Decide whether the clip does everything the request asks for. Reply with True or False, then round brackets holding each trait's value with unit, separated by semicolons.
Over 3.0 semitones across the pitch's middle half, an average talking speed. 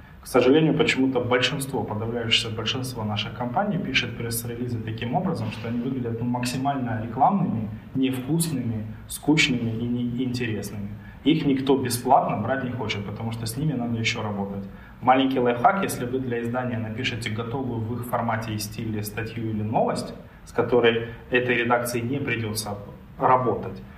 False (2.4 semitones; 145 wpm)